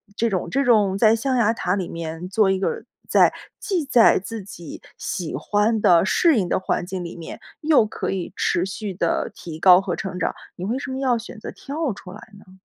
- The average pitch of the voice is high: Yes, high, 205 Hz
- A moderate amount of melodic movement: Yes, average, 4.5 semitones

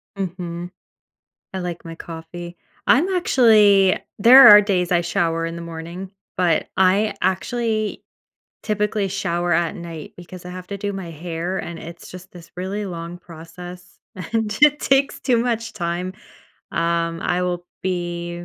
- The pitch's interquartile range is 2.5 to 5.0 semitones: Yes, average, 3.1 semitones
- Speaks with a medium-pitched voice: Yes, medium, 180 Hz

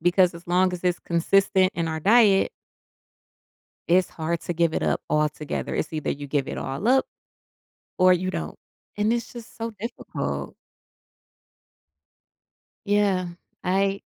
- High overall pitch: No, medium, 180 Hz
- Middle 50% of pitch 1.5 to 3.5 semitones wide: Yes, average, 2.9 semitones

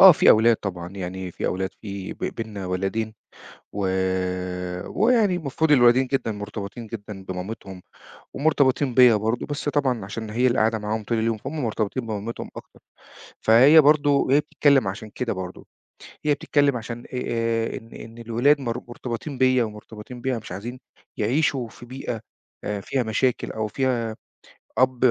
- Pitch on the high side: No, low, 115 Hz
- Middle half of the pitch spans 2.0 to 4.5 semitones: Yes, average, 3.7 semitones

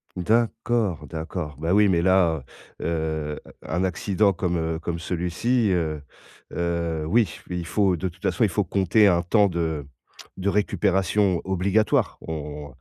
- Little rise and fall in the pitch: No, average, 3.5 semitones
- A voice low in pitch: Yes, very low, 90 Hz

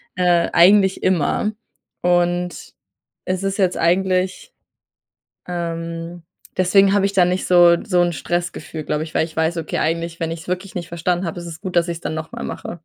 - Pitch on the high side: No, medium, 175 Hz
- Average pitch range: No, narrow, 1.7 semitones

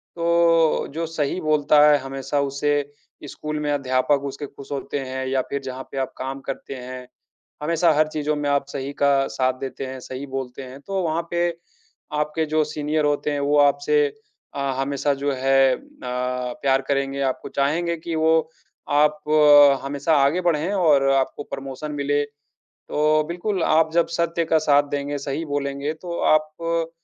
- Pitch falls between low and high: Yes, medium, 145 Hz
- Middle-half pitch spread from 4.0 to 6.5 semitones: No, narrow, 2.4 semitones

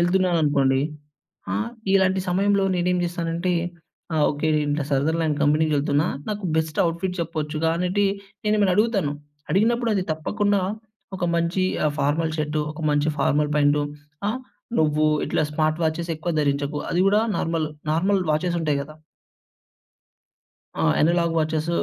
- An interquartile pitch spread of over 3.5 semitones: No, average, 3.2 semitones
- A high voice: No, medium, 165 Hz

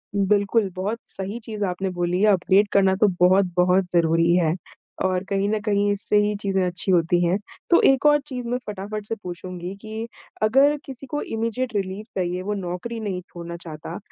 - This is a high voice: Yes, high, 195 Hz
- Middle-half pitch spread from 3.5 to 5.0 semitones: No, average, 3.1 semitones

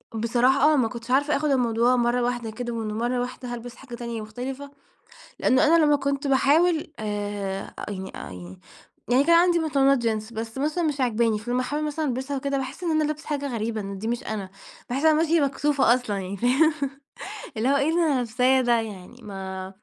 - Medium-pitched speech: No, very high, 250 Hz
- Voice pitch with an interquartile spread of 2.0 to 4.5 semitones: Yes, average, 4.0 semitones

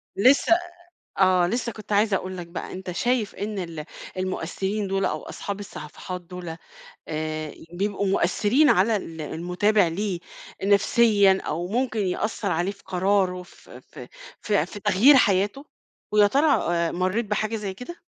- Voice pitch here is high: Yes, high, 195 Hz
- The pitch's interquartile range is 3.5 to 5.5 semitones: No, average, 2.9 semitones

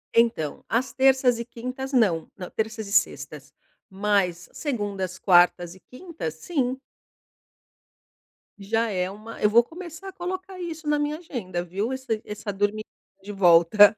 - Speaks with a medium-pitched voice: No, high, 220 Hz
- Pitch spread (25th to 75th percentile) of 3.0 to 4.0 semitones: No, wide, 5.4 semitones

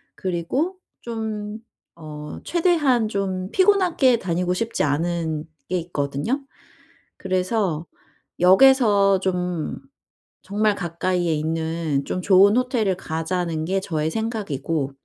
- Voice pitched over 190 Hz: No, medium, 185 Hz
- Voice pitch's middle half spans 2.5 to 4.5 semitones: No, average, 5.2 semitones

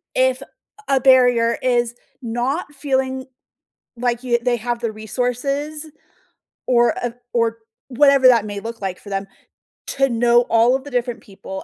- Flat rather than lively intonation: Yes, narrow, 2.2 semitones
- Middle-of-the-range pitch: No, high, 245 Hz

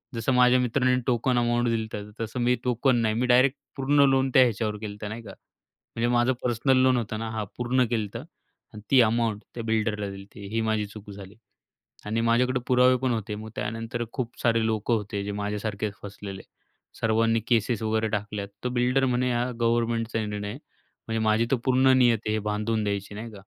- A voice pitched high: No, low, 115 Hz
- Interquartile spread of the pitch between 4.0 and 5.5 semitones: No, average, 2.7 semitones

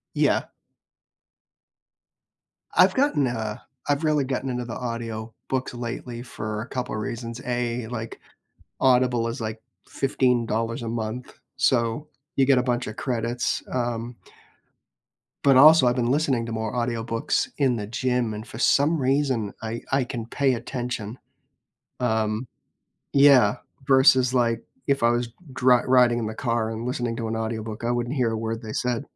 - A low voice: Yes, low, 120 Hz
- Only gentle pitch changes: Yes, narrow, 2.1 semitones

